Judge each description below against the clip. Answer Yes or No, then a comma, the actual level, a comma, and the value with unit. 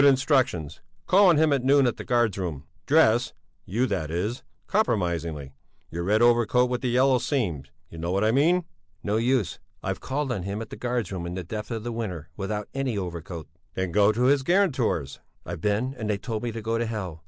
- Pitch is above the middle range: No, low, 110 Hz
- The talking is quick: Yes, fast, 210 wpm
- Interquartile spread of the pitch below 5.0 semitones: No, wide, 5.6 semitones